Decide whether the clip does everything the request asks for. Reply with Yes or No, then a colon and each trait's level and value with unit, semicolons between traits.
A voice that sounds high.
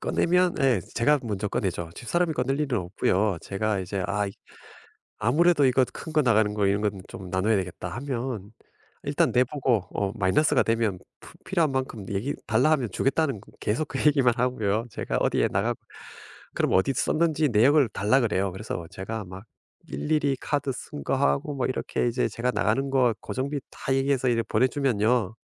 No: low, 120 Hz